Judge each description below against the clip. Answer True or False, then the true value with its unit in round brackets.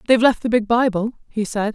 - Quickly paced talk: True (240 wpm)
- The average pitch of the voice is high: True (225 Hz)